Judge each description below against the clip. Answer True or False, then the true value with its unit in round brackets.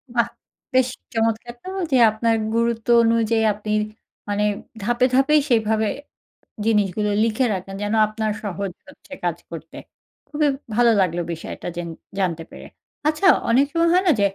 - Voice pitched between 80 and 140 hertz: False (225 Hz)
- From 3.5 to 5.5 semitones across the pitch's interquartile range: False (3.0 semitones)